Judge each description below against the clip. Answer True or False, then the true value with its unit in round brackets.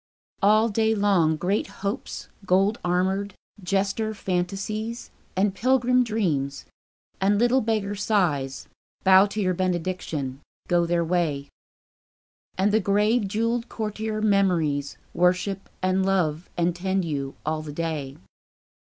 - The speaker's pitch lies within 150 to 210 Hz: True (190 Hz)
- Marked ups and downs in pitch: False (3.7 semitones)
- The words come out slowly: True (120 wpm)